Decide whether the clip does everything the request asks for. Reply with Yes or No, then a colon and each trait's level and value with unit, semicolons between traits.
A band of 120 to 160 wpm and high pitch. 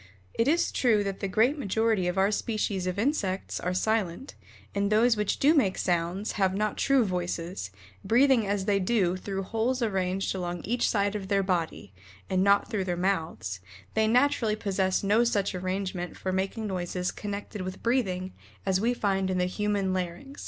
No: average, 180 wpm; high, 195 Hz